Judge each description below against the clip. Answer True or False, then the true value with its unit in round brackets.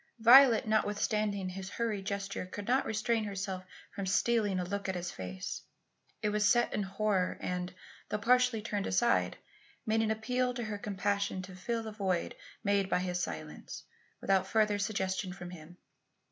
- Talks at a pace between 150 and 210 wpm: True (165 wpm)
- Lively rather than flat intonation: False (2.7 semitones)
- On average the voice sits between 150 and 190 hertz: False (200 Hz)